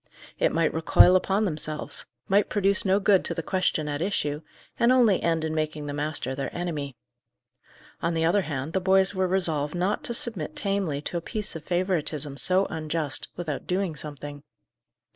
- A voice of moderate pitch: Yes, medium, 165 Hz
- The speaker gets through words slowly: No, average, 180 wpm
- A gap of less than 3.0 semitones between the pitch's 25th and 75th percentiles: No, average, 4.0 semitones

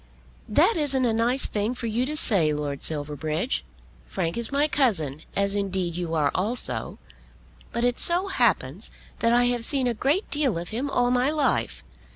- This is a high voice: Yes, high, 235 Hz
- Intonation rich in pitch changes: Yes, wide, 7.2 semitones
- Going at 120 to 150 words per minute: No, average, 180 wpm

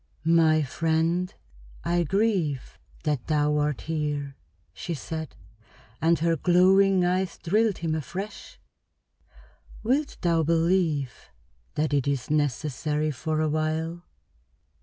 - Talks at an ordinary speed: No, slow, 110 wpm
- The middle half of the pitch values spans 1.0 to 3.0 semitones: Yes, average, 2.7 semitones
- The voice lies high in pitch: No, medium, 160 Hz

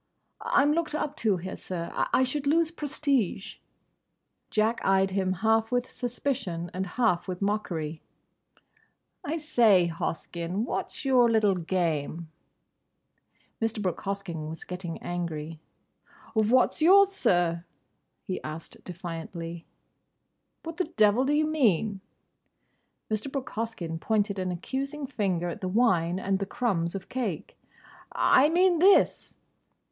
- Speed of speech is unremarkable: No, slow, 125 wpm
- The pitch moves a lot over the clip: Yes, wide, 6.7 semitones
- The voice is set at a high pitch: Yes, high, 200 Hz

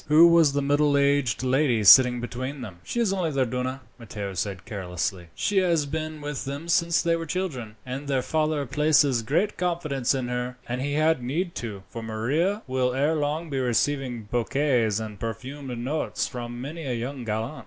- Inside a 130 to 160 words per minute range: No, average, 185 wpm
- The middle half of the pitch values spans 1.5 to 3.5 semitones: No, average, 4.2 semitones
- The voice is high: No, low, 135 Hz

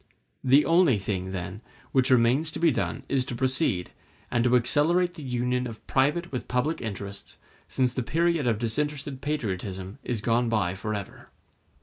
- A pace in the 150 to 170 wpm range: Yes, average, 160 wpm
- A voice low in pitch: Yes, low, 125 Hz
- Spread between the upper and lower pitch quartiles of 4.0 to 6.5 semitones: Yes, average, 5.1 semitones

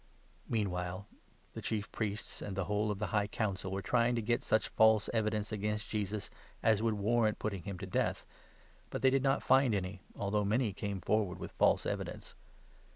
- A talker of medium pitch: No, low, 105 Hz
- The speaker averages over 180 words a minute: Yes, average, 195 wpm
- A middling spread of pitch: No, narrow, 1.9 semitones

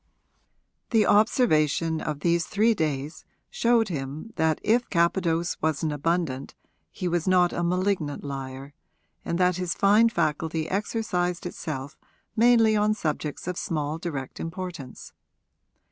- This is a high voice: No, medium, 170 Hz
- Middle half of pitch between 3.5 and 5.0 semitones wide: Yes, average, 4.6 semitones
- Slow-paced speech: Yes, slow, 130 wpm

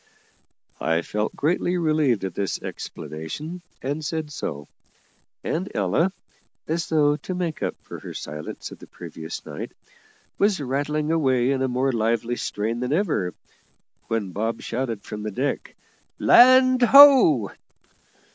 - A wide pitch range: Yes, wide, 7.1 semitones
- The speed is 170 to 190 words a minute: No, slow, 135 wpm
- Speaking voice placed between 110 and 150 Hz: Yes, low, 135 Hz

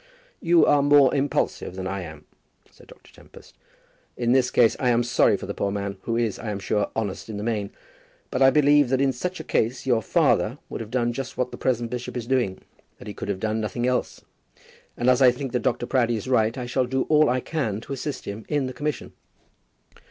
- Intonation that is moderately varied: Yes, average, 3.3 semitones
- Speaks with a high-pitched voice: No, low, 125 Hz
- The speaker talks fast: Yes, fast, 235 wpm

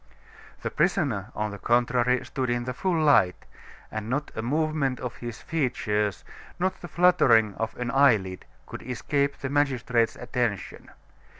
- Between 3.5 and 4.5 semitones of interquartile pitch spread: Yes, average, 4.2 semitones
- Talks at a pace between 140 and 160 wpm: Yes, average, 145 wpm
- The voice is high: No, low, 125 Hz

